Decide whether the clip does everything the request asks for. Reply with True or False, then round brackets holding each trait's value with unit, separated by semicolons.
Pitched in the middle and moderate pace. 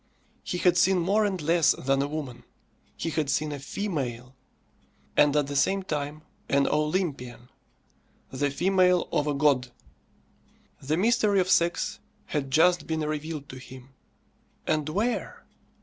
True (155 Hz; 145 wpm)